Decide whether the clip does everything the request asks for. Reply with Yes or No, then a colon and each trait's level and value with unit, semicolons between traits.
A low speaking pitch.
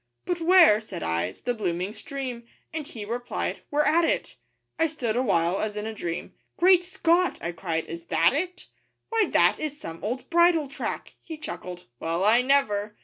No: high, 240 Hz